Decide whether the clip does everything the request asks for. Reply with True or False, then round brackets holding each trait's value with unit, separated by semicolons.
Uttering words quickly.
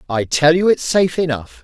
True (220 wpm)